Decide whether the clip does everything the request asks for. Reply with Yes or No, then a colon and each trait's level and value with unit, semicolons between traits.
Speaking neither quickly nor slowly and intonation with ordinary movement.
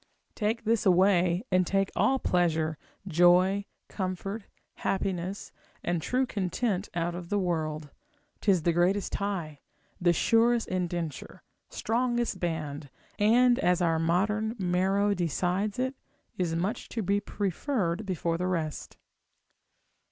No: slow, 120 wpm; average, 3.2 semitones